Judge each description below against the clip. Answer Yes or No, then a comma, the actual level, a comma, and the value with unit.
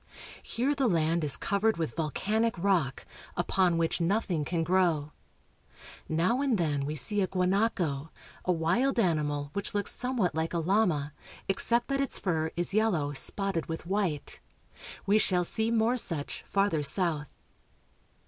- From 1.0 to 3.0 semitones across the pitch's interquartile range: No, average, 4.8 semitones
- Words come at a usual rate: Yes, average, 150 wpm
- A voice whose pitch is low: No, medium, 180 Hz